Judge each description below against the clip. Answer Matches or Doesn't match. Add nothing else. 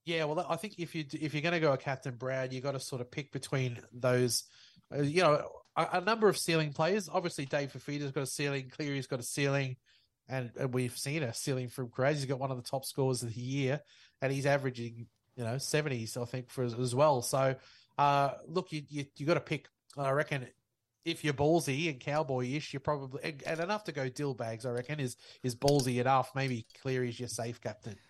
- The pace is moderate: Doesn't match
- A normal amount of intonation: Matches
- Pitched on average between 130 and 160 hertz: Matches